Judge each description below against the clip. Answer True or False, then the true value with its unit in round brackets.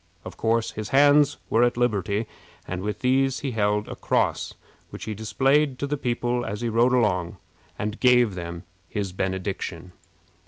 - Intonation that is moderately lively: True (3.9 semitones)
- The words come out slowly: False (165 wpm)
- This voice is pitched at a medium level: False (115 Hz)